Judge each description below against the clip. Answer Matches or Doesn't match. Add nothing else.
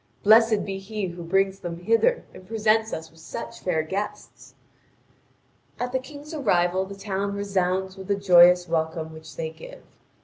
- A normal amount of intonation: Matches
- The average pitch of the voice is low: Doesn't match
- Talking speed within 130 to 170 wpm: Matches